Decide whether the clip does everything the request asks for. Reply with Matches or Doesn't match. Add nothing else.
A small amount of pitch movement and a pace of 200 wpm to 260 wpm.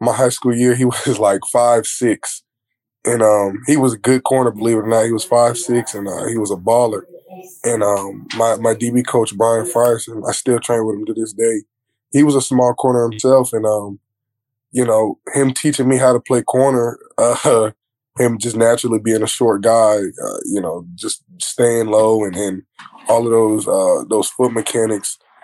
Matches